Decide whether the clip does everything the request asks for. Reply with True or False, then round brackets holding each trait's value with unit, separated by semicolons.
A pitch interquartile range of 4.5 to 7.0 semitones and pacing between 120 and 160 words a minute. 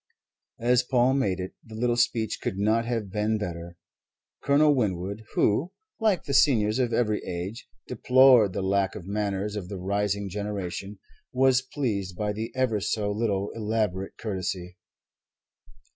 False (3.6 semitones; 145 wpm)